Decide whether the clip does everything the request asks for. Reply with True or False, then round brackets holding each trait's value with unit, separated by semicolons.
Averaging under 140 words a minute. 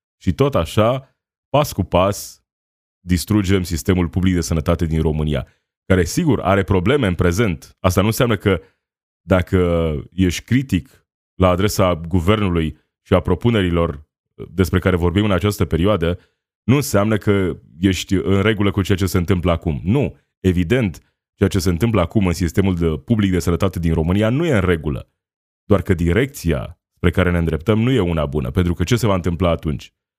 False (170 wpm)